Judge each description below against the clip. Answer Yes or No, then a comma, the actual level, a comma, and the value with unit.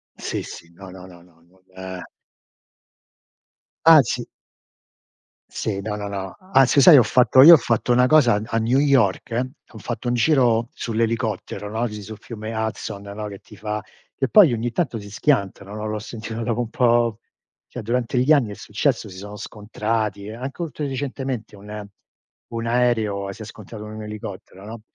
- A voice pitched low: Yes, low, 110 Hz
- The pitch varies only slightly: No, average, 3.0 semitones